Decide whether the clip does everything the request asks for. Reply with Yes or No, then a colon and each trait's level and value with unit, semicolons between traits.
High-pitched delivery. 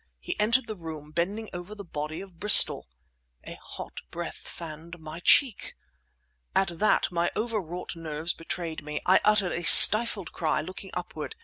No: medium, 175 Hz